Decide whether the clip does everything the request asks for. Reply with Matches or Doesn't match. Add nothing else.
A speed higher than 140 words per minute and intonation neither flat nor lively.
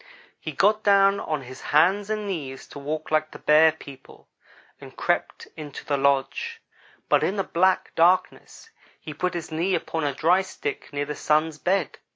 Matches